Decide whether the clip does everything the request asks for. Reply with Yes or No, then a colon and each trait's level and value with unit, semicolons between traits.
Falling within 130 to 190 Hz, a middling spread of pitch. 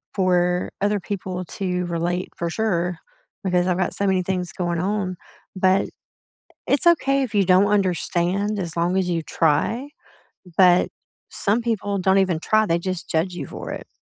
No: medium, 185 Hz; narrow, 2.3 semitones